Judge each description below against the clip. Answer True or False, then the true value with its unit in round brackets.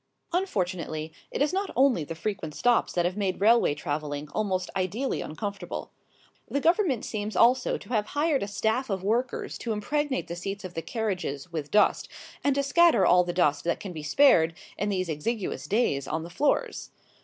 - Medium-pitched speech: False (200 Hz)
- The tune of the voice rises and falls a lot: True (6.3 semitones)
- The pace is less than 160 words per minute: False (185 wpm)